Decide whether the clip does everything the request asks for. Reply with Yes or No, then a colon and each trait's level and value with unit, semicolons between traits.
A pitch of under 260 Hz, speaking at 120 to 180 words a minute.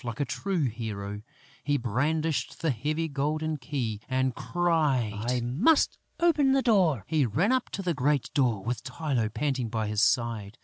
Yes: low, 135 Hz; average, 170 wpm